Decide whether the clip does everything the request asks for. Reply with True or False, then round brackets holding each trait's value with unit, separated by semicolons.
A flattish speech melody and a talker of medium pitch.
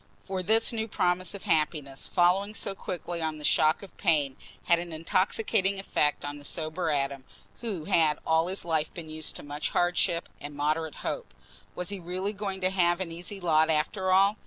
False (3.6 semitones; 175 Hz)